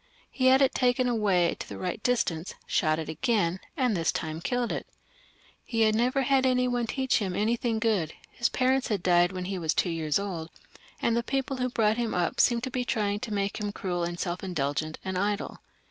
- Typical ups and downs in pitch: No, wide, 5.8 semitones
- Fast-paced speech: Yes, fast, 225 wpm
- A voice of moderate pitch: No, high, 210 Hz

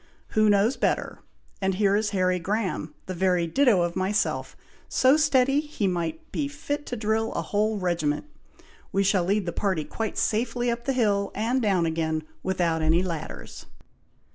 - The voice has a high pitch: Yes, high, 200 Hz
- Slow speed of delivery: No, average, 165 wpm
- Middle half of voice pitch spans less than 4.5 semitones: No, average, 4.8 semitones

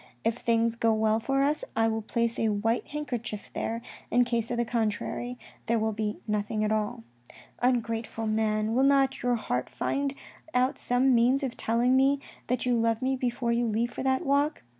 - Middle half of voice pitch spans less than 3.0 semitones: Yes, narrow, 2.5 semitones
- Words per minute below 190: No, average, 195 wpm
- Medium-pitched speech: No, high, 235 Hz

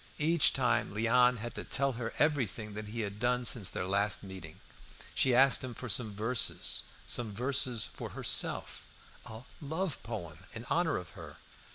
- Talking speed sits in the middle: Yes, average, 170 wpm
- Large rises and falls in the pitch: No, average, 3.6 semitones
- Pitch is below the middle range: Yes, low, 115 Hz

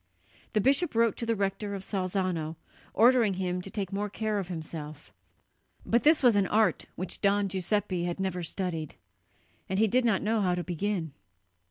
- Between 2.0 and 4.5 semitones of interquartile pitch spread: Yes, average, 3.2 semitones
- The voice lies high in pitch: Yes, high, 195 Hz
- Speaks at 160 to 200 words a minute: Yes, average, 180 wpm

